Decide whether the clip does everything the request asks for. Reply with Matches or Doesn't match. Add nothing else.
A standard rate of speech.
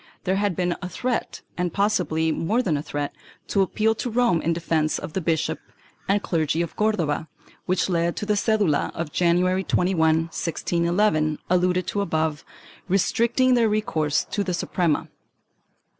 Matches